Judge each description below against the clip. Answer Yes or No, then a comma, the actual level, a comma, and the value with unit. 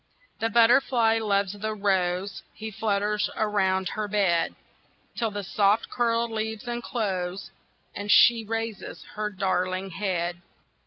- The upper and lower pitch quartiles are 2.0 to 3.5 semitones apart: Yes, narrow, 2.6 semitones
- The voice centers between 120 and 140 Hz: No, high, 210 Hz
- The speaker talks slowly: Yes, slow, 120 wpm